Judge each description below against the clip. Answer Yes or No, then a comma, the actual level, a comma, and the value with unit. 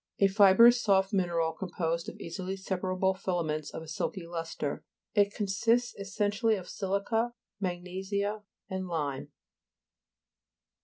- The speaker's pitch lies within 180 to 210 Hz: Yes, high, 190 Hz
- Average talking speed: No, slow, 120 wpm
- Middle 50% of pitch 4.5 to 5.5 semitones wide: No, average, 2.8 semitones